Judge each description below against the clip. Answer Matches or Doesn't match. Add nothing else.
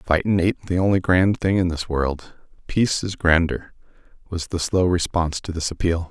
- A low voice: Matches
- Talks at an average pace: Matches